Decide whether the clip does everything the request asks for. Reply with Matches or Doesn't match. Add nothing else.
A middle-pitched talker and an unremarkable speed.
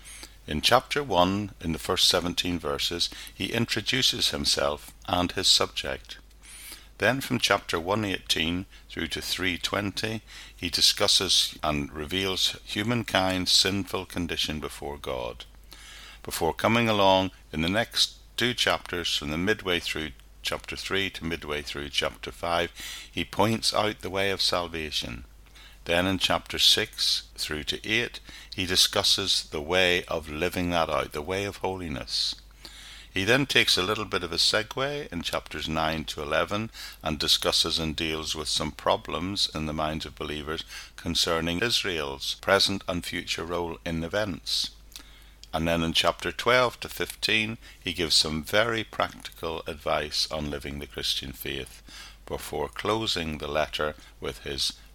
Doesn't match